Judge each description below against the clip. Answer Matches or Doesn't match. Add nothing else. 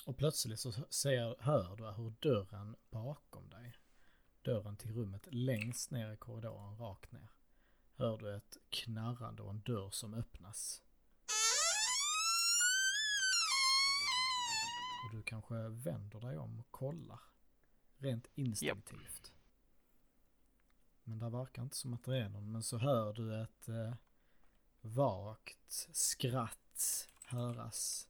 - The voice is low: Matches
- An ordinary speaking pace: Doesn't match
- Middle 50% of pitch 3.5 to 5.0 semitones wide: Matches